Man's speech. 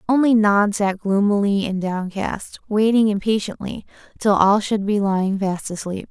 No: female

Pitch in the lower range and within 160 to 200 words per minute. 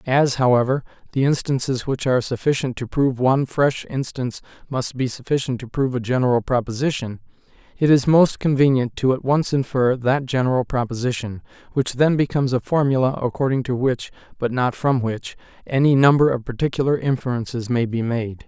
Yes: low, 130 Hz; average, 165 wpm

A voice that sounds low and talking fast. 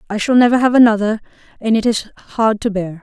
No: high, 220 Hz; fast, 220 wpm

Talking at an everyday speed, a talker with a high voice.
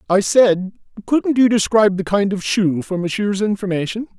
Yes: average, 170 wpm; high, 200 Hz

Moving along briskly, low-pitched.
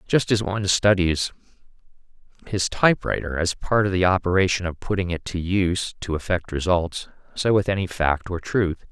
No: average, 170 wpm; very low, 90 Hz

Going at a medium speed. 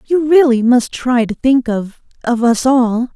Yes: average, 170 wpm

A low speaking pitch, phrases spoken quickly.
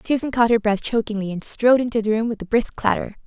No: high, 225 Hz; fast, 255 wpm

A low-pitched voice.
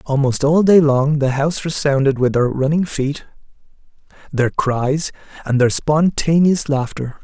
No: medium, 145 Hz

